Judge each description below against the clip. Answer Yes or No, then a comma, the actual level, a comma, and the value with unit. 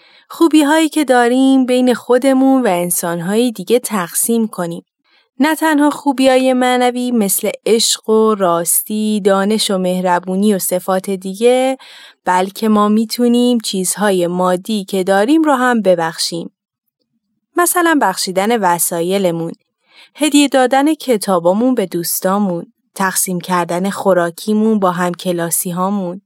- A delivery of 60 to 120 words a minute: Yes, average, 115 wpm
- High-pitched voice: Yes, high, 210 Hz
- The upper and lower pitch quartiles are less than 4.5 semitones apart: No, wide, 5.4 semitones